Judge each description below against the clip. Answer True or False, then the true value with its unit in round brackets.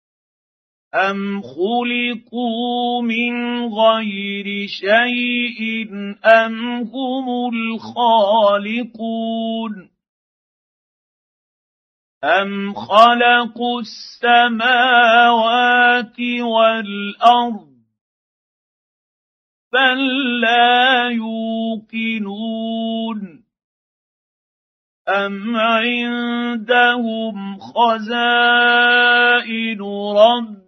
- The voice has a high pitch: True (230 Hz)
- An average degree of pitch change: False (1.4 semitones)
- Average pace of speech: False (35 wpm)